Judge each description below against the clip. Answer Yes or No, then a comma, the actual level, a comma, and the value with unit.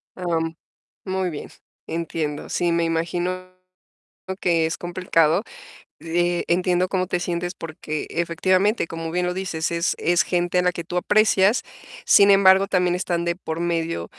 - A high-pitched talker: No, medium, 175 Hz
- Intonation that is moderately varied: No, narrow, 1.7 semitones